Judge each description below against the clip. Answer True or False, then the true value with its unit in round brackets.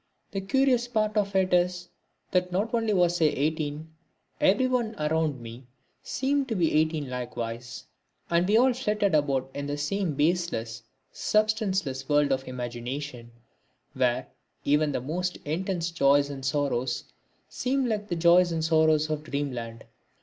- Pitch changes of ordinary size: False (5.9 semitones)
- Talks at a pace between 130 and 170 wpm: True (150 wpm)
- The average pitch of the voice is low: False (160 Hz)